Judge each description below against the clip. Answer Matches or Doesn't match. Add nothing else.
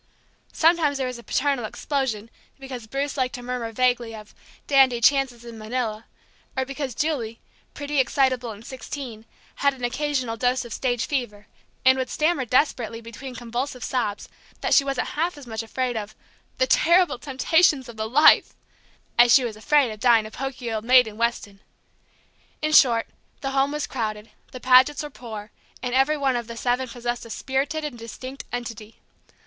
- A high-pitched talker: Matches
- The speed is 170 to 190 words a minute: Matches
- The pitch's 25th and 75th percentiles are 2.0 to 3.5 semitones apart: Matches